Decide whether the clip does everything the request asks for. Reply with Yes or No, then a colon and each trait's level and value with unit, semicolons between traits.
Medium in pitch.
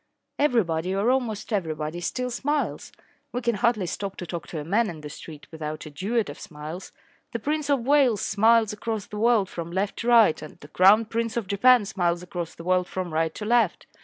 No: high, 200 Hz